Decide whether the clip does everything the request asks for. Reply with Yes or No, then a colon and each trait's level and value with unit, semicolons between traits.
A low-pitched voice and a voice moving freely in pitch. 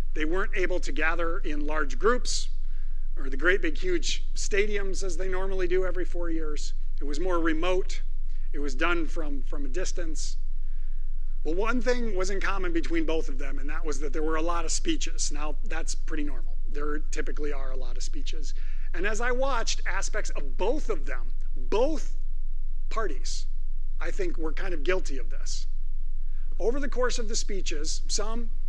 No: medium, 180 Hz; wide, 6.9 semitones